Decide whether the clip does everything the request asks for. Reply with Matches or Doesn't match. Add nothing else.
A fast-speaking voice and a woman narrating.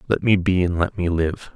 Doesn't match